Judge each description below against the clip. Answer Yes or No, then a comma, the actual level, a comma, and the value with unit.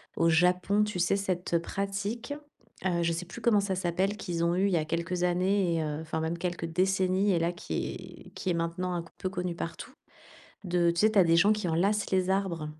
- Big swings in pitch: No, narrow, 2.4 semitones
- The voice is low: No, medium, 180 Hz